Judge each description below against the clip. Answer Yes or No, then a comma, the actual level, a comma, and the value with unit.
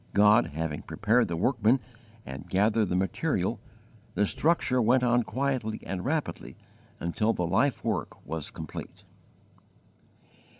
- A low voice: Yes, low, 110 Hz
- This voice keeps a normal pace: No, slow, 125 wpm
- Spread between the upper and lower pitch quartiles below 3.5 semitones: No, wide, 5.6 semitones